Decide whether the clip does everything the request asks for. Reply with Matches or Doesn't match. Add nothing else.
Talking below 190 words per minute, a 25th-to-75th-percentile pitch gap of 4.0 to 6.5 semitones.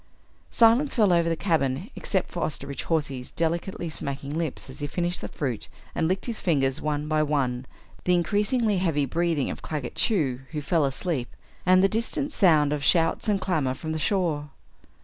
Matches